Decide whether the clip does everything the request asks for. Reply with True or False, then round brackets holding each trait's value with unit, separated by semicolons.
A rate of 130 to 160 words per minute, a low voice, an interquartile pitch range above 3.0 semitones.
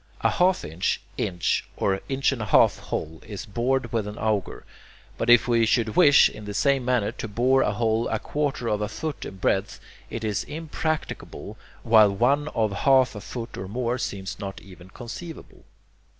False (185 wpm; 115 Hz; 4.3 semitones)